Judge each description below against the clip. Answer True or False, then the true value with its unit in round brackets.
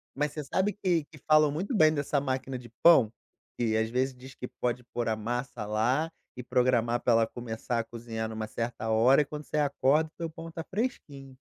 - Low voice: True (130 Hz)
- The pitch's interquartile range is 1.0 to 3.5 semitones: False (4.6 semitones)